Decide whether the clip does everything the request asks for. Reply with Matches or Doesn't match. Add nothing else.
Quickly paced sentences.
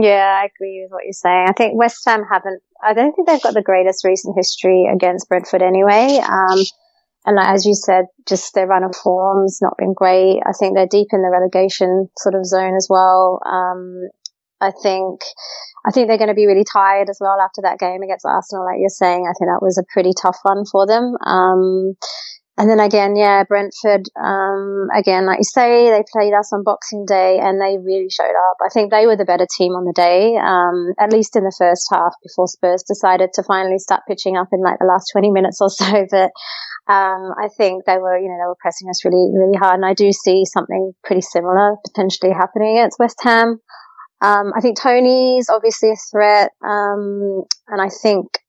Matches